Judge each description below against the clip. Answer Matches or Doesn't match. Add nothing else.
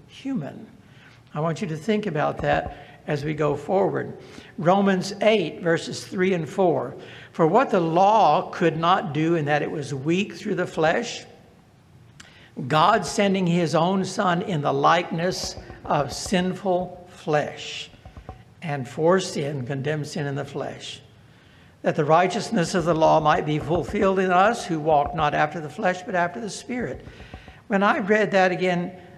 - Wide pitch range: Doesn't match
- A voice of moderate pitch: Matches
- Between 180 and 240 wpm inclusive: Doesn't match